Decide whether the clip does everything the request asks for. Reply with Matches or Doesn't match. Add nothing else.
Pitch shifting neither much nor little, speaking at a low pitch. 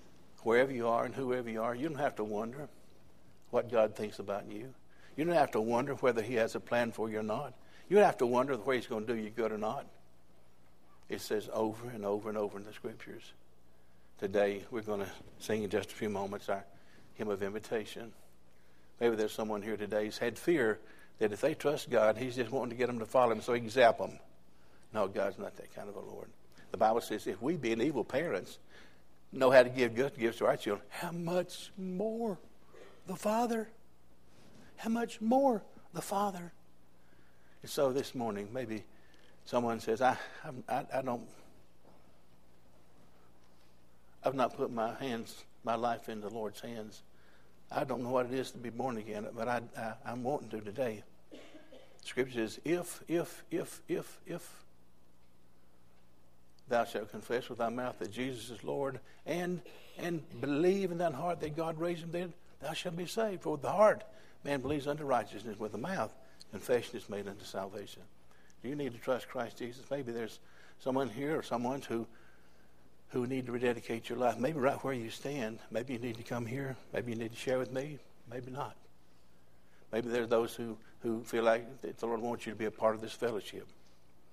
Doesn't match